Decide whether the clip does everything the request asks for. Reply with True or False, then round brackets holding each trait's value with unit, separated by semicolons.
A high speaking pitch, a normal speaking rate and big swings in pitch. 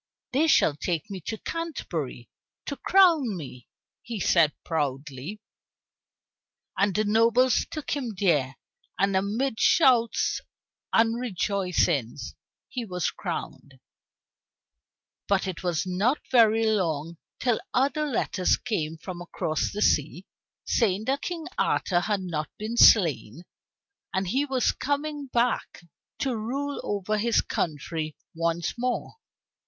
False (205 Hz; 125 wpm; 6.7 semitones)